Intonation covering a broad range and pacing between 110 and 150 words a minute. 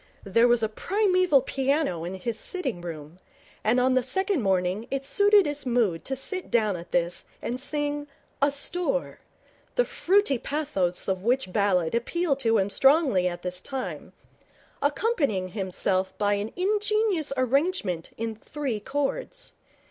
Yes: wide, 7.6 semitones; average, 145 wpm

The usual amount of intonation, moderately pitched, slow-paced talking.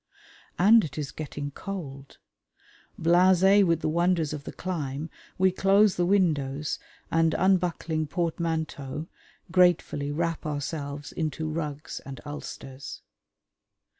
Yes: average, 3.6 semitones; medium, 160 Hz; slow, 110 wpm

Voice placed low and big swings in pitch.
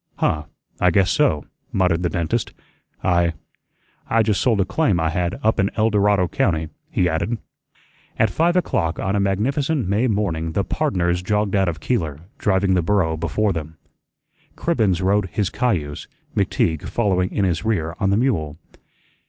No: very low, 95 Hz; average, 4.2 semitones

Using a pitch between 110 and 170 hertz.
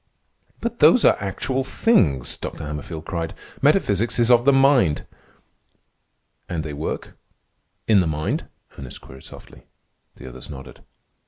No: very low, 90 Hz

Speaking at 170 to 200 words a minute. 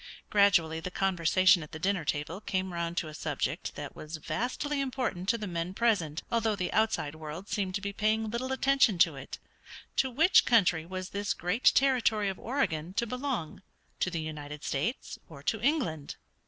Yes: average, 180 wpm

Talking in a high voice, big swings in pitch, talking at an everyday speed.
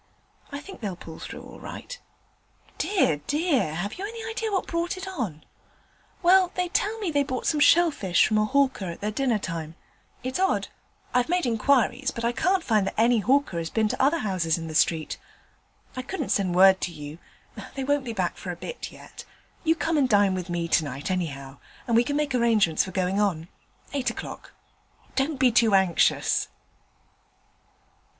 Yes: high, 235 Hz; wide, 8.3 semitones; average, 190 wpm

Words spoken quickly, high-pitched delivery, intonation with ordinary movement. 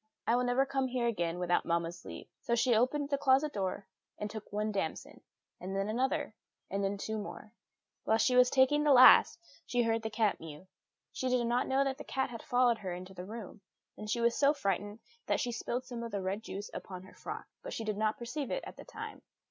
Yes: fast, 230 wpm; high, 230 Hz; average, 4.2 semitones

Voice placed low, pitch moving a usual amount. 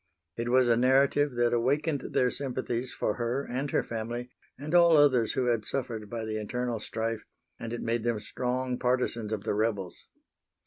No: low, 120 Hz; narrow, 2.3 semitones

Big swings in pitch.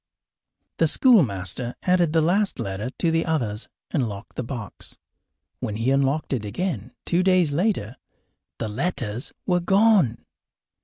Yes: wide, 8.1 semitones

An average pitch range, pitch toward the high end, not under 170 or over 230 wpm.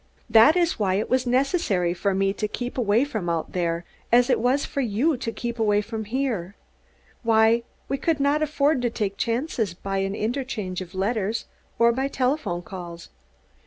Yes: average, 5.0 semitones; high, 225 Hz; average, 180 wpm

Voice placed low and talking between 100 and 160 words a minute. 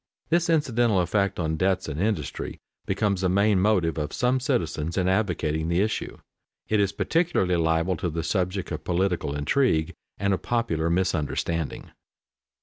Yes: very low, 95 Hz; average, 155 wpm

